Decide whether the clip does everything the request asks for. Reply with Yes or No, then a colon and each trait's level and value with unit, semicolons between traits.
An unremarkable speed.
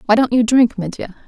No: fast, 235 wpm